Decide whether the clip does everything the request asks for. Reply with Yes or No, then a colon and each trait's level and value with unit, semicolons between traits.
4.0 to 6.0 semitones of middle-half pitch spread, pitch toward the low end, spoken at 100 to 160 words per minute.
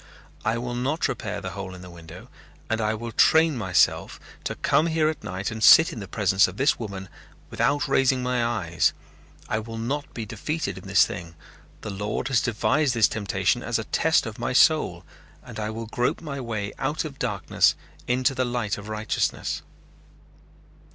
No: average, 4.5 semitones; low, 115 Hz; average, 185 wpm